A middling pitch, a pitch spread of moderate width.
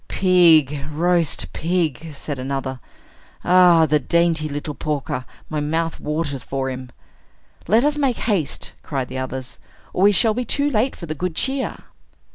Yes: medium, 160 Hz; average, 4.7 semitones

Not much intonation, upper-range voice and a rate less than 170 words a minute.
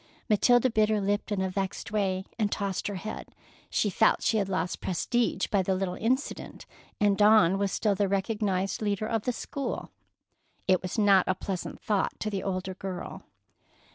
No: narrow, 2.2 semitones; high, 200 Hz; average, 180 wpm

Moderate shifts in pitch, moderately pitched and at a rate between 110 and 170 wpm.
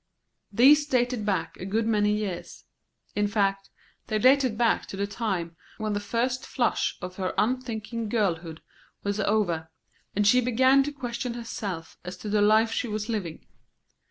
No: average, 3.3 semitones; high, 215 Hz; average, 160 wpm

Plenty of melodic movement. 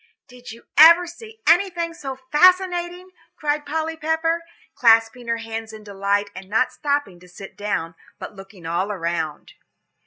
Yes: wide, 8.6 semitones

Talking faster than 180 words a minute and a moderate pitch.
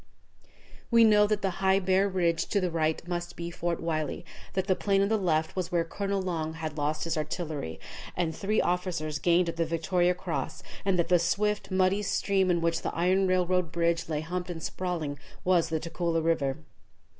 Yes: average, 190 wpm; medium, 175 Hz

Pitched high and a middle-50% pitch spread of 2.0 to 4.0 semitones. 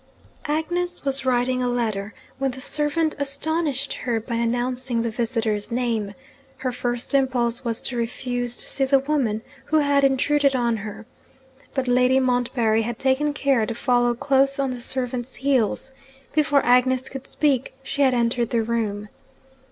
Yes: very high, 250 Hz; average, 2.7 semitones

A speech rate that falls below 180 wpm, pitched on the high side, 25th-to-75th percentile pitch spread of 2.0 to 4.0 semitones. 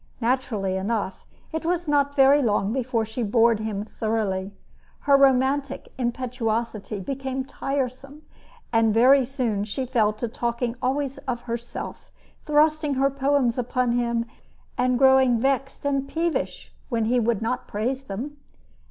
Yes: slow, 135 wpm; very high, 250 Hz; average, 3.2 semitones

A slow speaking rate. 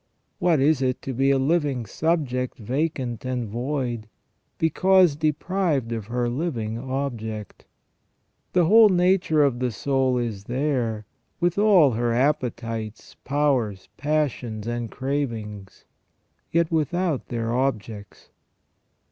Yes: slow, 115 wpm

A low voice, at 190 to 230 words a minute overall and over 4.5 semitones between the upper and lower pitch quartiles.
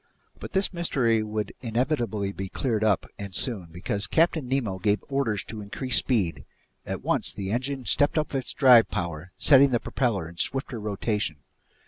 No: low, 110 Hz; average, 165 wpm; average, 5.0 semitones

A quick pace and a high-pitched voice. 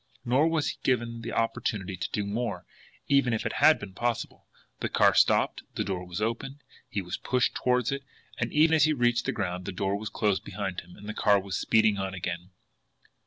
No: fast, 210 wpm; low, 110 Hz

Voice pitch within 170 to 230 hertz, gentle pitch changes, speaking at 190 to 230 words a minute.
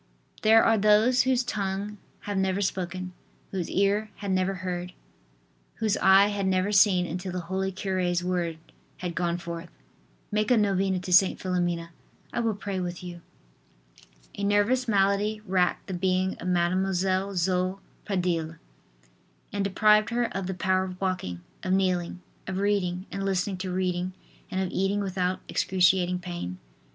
No: high, 190 Hz; narrow, 1.8 semitones; average, 155 wpm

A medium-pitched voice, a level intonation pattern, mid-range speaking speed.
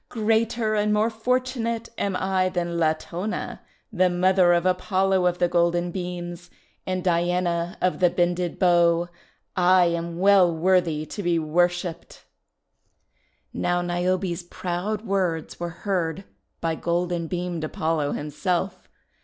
No: medium, 175 Hz; narrow, 1.7 semitones; slow, 125 wpm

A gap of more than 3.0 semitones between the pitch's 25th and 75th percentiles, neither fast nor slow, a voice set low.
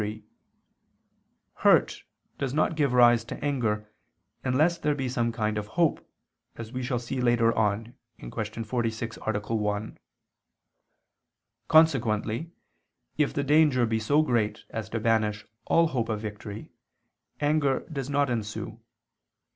No: average, 4.4 semitones; slow, 130 wpm; low, 120 Hz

